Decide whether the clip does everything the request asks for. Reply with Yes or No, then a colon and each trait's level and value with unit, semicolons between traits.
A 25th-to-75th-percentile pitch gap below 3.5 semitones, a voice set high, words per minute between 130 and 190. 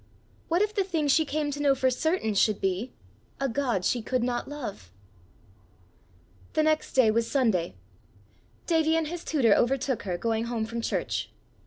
No: average, 5.3 semitones; very high, 260 Hz; average, 170 wpm